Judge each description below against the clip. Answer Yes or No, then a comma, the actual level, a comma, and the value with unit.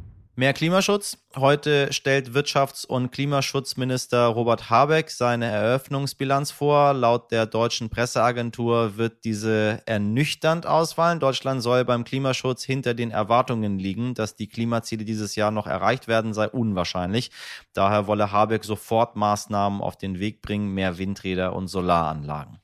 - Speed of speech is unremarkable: Yes, average, 135 wpm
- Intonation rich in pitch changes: No, average, 4.2 semitones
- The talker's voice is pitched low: Yes, low, 115 Hz